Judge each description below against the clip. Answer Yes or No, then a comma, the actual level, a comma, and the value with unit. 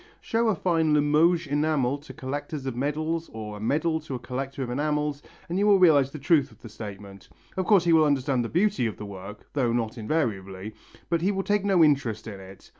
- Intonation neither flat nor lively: No, wide, 5.9 semitones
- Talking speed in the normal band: No, fast, 225 wpm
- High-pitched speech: No, medium, 145 Hz